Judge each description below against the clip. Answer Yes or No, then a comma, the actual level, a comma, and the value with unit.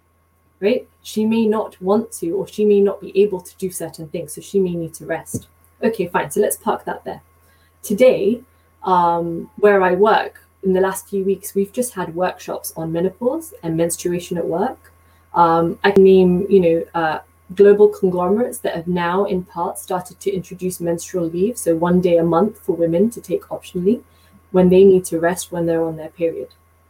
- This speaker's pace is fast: No, average, 195 wpm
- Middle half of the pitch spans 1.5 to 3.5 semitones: Yes, average, 3.1 semitones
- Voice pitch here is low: No, medium, 180 Hz